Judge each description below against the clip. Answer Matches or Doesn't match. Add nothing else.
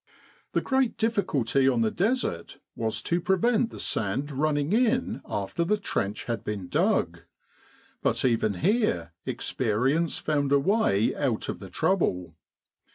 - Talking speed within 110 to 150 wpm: Matches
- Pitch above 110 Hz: Matches